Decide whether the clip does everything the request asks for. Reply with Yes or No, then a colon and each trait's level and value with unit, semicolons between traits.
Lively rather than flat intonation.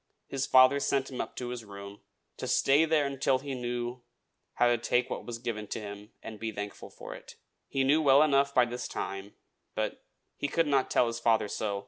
No: average, 3.5 semitones